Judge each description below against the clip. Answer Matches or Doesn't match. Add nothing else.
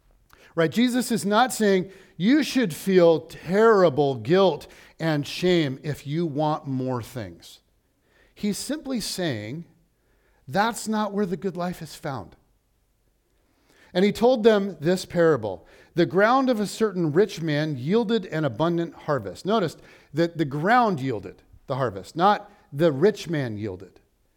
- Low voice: Doesn't match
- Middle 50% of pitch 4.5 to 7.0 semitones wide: Matches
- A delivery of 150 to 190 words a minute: Doesn't match